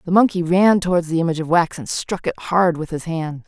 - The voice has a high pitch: No, medium, 170 Hz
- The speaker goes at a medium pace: No, fast, 260 wpm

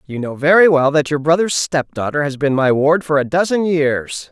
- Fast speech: Yes, fast, 225 wpm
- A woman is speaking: No, male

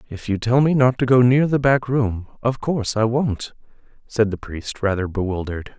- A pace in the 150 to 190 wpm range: No, fast, 205 wpm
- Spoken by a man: Yes, male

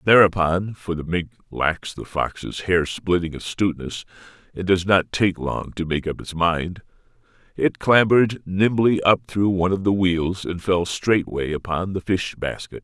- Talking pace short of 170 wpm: Yes, average, 160 wpm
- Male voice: Yes, male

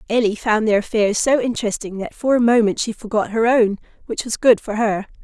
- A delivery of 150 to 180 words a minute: No, fast, 205 wpm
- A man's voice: No, female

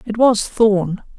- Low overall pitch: No, high, 210 Hz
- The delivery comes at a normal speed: Yes, average, 150 wpm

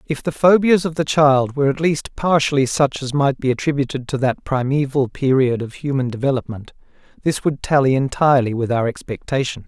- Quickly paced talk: No, average, 180 wpm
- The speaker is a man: Yes, male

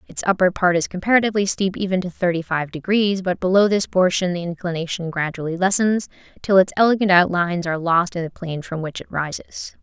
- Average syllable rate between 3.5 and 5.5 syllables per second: No, 5.9 syllables/s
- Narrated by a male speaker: No, female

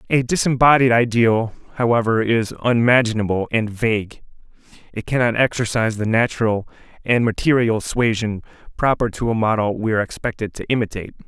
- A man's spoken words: Yes, male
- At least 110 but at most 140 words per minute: Yes, slow, 135 wpm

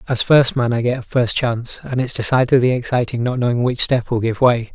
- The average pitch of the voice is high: No, low, 120 Hz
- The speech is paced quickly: Yes, fast, 230 wpm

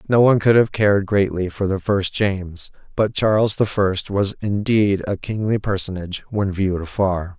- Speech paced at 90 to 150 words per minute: No, average, 180 wpm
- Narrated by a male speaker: Yes, male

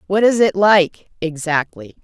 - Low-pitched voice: No, medium, 180 Hz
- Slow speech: Yes, slow, 120 wpm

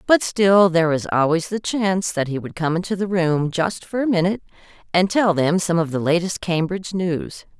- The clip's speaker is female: Yes, female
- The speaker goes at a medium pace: No, fast, 215 wpm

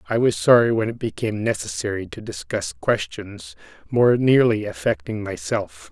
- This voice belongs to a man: Yes, male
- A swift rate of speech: No, average, 140 wpm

